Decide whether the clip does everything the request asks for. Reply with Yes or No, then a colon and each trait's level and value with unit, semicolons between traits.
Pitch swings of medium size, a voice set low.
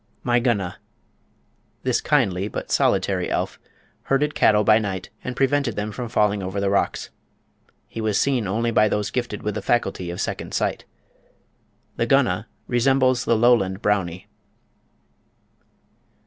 Yes: average, 3.7 semitones; low, 105 Hz